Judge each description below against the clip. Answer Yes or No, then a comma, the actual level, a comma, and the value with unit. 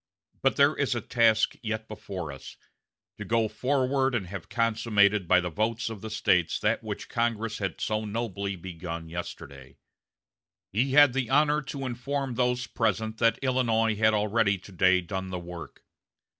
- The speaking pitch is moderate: No, low, 110 Hz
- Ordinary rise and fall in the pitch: Yes, average, 4.3 semitones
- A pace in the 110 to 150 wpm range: No, average, 165 wpm